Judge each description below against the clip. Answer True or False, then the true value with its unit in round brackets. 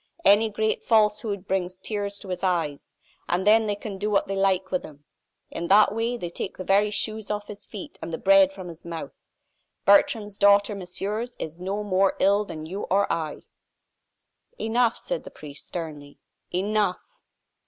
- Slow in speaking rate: False (175 wpm)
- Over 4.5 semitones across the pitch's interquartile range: False (2.6 semitones)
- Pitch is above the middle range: True (200 Hz)